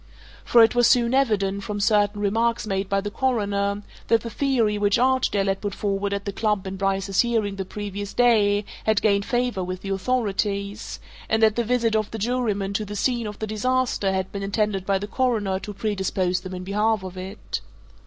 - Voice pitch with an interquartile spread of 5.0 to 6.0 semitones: No, narrow, 2.5 semitones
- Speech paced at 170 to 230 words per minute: Yes, fast, 205 wpm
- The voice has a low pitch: No, high, 205 Hz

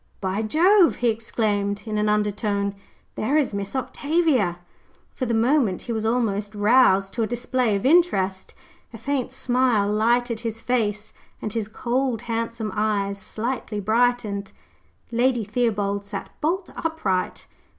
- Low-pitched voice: No, high, 225 Hz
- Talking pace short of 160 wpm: Yes, average, 140 wpm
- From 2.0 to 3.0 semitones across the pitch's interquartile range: No, average, 3.4 semitones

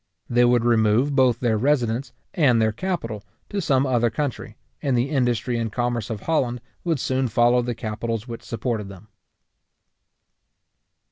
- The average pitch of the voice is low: Yes, low, 120 Hz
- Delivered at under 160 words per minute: Yes, average, 150 wpm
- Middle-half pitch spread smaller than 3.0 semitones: Yes, narrow, 2.6 semitones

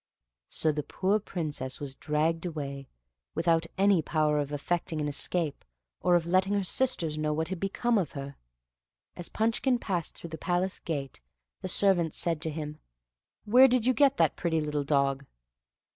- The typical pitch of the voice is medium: Yes, medium, 165 Hz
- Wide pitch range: No, average, 4.1 semitones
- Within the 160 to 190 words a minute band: Yes, average, 170 wpm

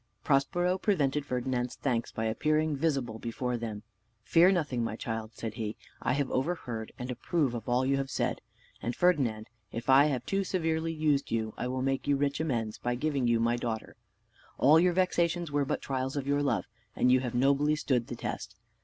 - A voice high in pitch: No, low, 135 Hz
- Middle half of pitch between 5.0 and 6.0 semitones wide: No, average, 4.2 semitones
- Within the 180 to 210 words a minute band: Yes, average, 195 wpm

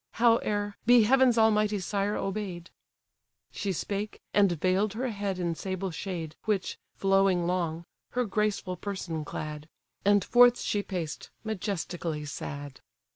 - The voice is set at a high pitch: Yes, high, 195 Hz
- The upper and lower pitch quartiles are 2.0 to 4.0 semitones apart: Yes, average, 3.5 semitones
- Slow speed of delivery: Yes, slow, 130 wpm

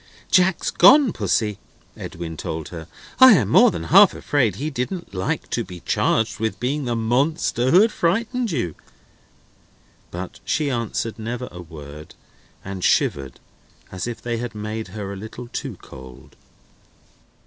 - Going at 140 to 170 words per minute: Yes, average, 150 wpm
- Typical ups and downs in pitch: No, wide, 7.8 semitones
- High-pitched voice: No, low, 115 Hz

